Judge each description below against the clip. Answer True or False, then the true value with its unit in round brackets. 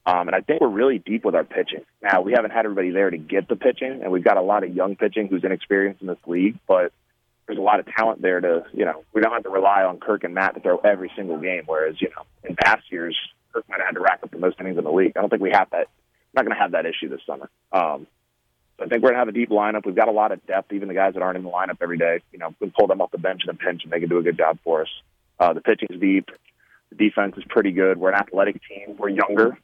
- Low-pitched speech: True (95 Hz)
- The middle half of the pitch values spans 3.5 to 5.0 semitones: False (2.5 semitones)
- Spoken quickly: True (315 wpm)